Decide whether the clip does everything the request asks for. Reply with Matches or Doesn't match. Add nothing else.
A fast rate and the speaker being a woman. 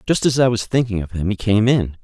Doesn't match